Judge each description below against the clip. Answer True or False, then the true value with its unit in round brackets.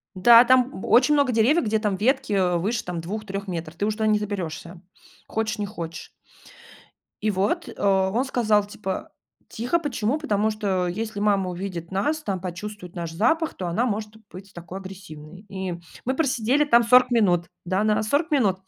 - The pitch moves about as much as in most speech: True (4.0 semitones)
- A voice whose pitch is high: True (210 Hz)